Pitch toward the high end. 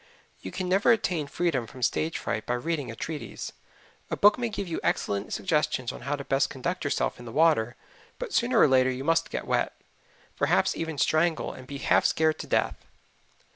No: medium, 150 Hz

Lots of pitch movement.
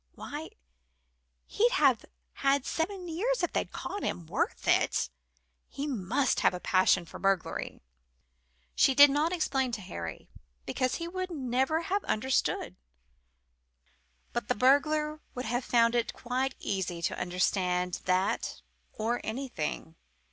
Yes: wide, 7.7 semitones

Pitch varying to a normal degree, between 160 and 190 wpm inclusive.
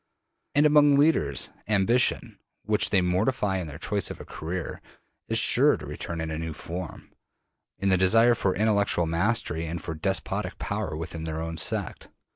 Yes: average, 4.9 semitones; average, 170 wpm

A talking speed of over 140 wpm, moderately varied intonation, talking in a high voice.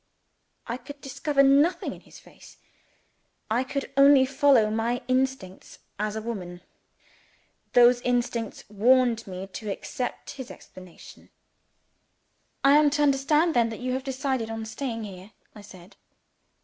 No: slow, 135 wpm; average, 4.0 semitones; high, 245 Hz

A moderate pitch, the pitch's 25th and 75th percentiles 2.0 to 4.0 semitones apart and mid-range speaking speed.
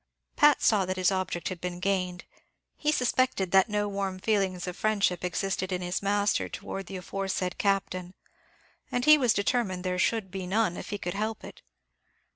No: high, 195 Hz; narrow, 2.4 semitones; average, 180 wpm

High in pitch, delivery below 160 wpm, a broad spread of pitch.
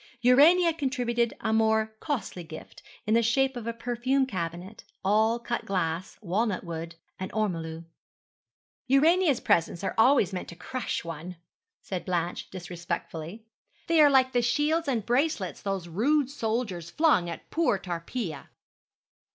Yes: high, 220 Hz; average, 140 wpm; wide, 6.7 semitones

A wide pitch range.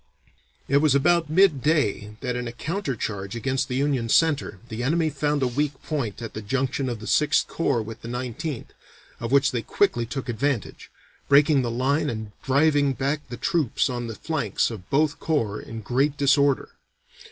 No: average, 3.9 semitones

